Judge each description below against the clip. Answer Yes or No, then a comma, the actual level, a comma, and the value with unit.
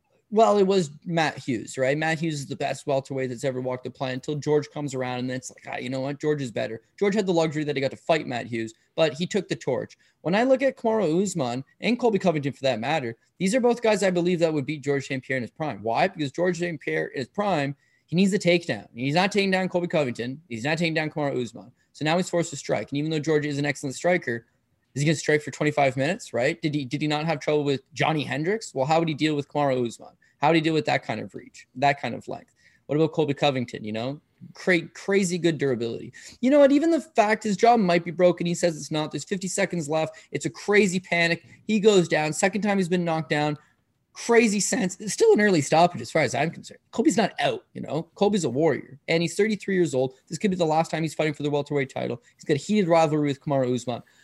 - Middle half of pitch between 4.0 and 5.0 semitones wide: Yes, average, 4.6 semitones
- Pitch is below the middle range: No, medium, 155 Hz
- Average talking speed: No, fast, 265 wpm